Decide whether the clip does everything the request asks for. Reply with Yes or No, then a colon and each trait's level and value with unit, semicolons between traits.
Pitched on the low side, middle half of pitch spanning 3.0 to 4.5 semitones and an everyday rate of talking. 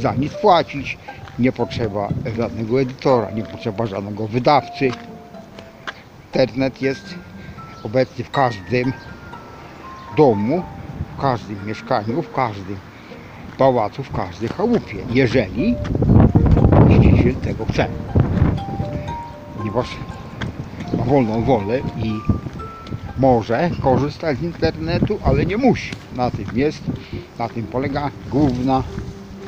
No: low, 120 Hz; average, 4.0 semitones; slow, 100 wpm